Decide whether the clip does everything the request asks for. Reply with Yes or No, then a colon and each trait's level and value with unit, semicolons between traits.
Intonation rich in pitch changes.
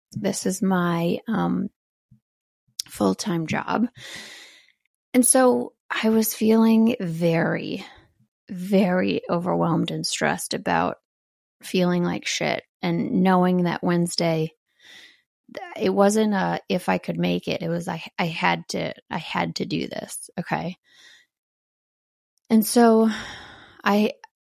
No: average, 4.7 semitones